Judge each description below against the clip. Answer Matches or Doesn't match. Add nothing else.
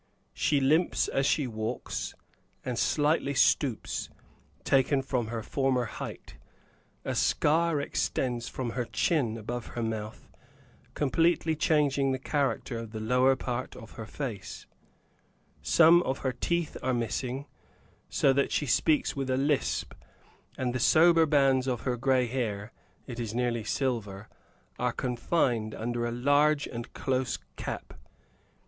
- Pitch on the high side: Doesn't match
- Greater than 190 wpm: Doesn't match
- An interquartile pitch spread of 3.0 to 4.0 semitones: Matches